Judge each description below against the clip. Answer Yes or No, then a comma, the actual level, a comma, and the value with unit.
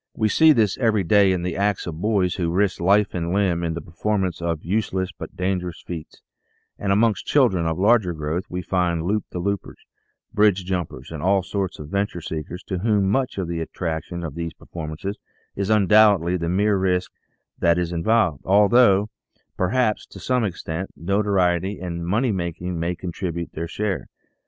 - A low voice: Yes, very low, 95 Hz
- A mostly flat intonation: No, average, 3.1 semitones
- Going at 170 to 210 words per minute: Yes, average, 175 wpm